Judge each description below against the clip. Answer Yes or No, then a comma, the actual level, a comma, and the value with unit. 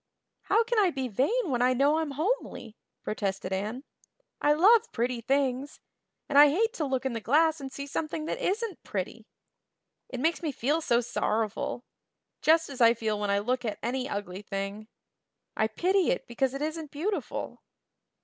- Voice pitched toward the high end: Yes, very high, 270 Hz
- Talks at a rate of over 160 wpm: Yes, average, 180 wpm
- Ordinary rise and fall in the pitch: No, wide, 5.8 semitones